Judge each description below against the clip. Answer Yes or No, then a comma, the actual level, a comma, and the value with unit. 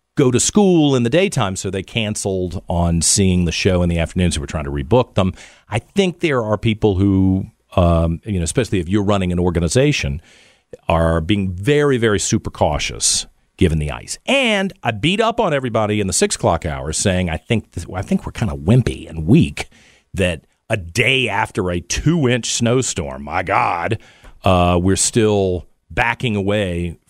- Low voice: Yes, low, 100 Hz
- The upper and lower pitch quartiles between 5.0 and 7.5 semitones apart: Yes, average, 5.3 semitones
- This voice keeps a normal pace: Yes, average, 180 wpm